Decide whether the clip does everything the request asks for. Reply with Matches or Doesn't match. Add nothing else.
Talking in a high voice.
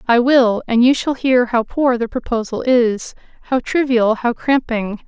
Matches